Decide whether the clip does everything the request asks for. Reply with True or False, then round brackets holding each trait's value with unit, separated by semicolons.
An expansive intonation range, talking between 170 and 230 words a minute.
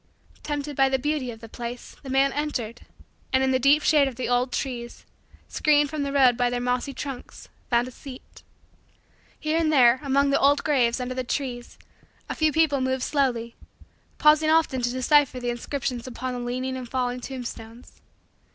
False (2.6 semitones; 185 wpm)